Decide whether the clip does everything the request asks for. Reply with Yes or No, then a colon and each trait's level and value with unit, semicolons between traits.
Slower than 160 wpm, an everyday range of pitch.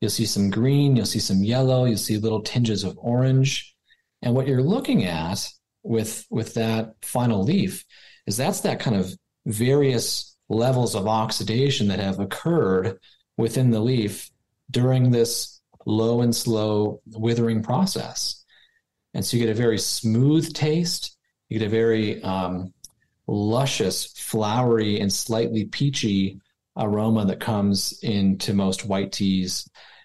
Yes: average, 140 wpm; average, 3.1 semitones